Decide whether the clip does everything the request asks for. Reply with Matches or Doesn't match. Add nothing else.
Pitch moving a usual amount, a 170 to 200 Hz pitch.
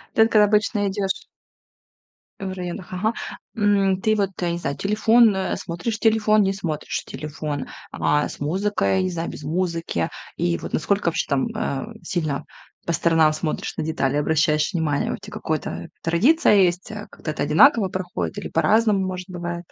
Matches